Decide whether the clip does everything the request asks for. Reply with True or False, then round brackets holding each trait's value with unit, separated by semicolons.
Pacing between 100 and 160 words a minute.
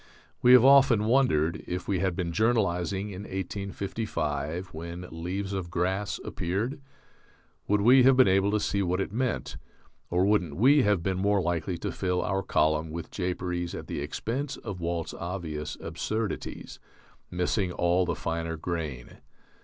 True (155 wpm)